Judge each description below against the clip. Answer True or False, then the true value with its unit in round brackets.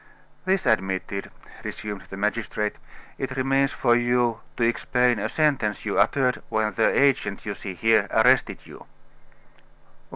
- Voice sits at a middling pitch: False (115 Hz)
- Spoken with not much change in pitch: False (3.5 semitones)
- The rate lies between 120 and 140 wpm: True (135 wpm)